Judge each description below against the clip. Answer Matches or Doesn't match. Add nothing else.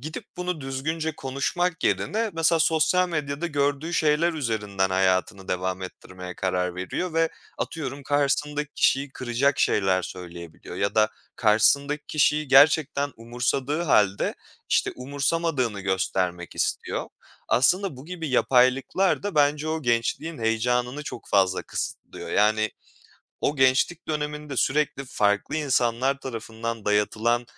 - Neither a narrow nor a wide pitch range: Doesn't match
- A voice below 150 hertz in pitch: Matches